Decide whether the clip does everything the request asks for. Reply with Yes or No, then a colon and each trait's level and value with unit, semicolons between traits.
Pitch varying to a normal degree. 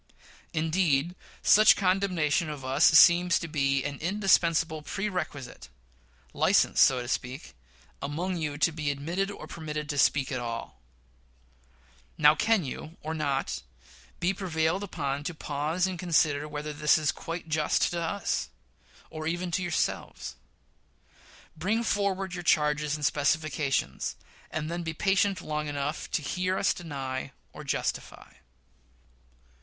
Yes: average, 3.4 semitones